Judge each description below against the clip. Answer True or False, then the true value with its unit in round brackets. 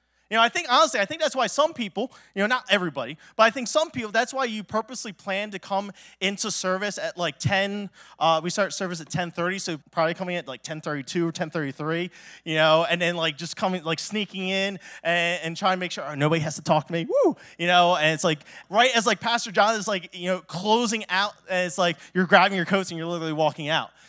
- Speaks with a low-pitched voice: False (185 Hz)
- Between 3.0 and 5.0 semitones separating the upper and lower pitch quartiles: True (4.1 semitones)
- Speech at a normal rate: False (245 wpm)